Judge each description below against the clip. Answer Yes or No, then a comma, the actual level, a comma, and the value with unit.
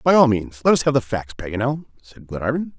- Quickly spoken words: Yes, fast, 235 wpm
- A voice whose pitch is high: No, low, 125 Hz